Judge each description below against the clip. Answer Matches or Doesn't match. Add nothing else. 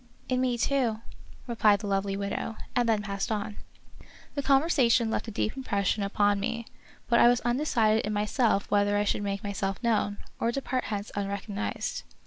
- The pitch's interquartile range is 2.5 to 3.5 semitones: Matches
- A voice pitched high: Matches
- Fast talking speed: Doesn't match